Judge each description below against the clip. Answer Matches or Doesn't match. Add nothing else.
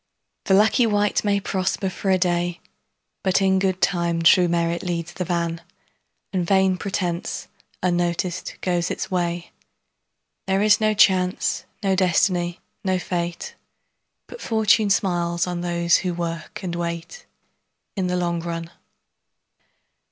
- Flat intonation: Matches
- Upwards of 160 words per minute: Doesn't match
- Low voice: Doesn't match